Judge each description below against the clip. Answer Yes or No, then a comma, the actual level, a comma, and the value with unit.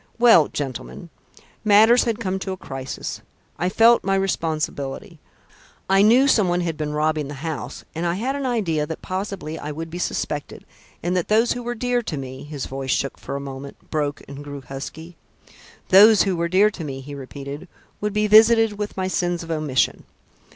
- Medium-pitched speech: Yes, medium, 170 Hz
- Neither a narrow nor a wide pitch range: No, wide, 6.3 semitones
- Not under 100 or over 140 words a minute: No, average, 190 wpm